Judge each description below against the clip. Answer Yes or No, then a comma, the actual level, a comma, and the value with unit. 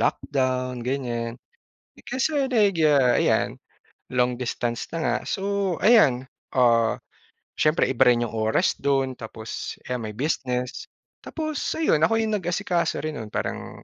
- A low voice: Yes, low, 130 Hz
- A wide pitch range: Yes, wide, 6.7 semitones